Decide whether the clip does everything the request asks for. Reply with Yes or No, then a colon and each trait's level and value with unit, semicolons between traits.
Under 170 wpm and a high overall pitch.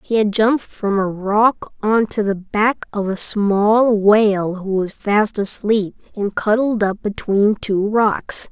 Yes: average, 160 wpm; high, 210 Hz